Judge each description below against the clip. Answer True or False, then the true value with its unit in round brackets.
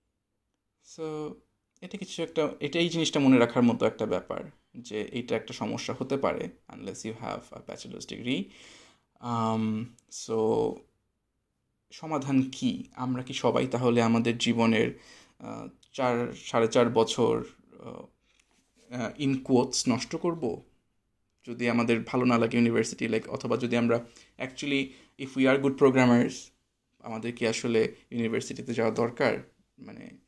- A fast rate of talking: True (125 wpm)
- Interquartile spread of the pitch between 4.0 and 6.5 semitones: False (3.0 semitones)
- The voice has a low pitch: True (120 Hz)